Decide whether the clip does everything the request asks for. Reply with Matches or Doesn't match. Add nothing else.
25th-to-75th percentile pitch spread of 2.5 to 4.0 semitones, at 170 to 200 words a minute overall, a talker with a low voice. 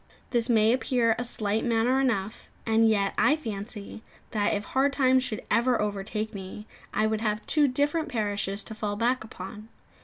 Doesn't match